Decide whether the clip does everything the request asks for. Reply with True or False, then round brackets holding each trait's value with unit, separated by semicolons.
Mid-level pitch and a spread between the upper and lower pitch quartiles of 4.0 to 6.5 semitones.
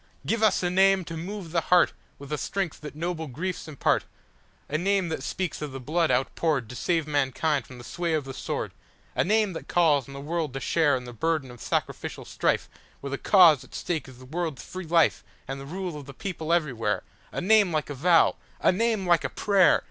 True (160 Hz; 4.4 semitones)